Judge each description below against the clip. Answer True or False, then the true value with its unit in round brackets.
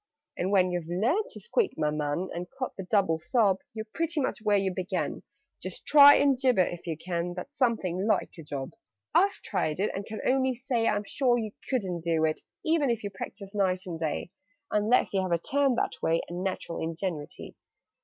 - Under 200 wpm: False (205 wpm)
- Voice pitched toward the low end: False (195 Hz)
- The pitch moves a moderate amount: False (6.0 semitones)